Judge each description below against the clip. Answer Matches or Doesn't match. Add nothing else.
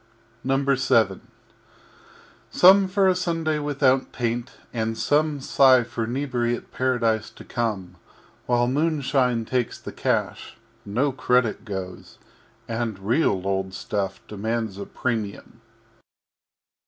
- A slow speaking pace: Matches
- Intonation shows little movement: Doesn't match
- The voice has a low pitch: Matches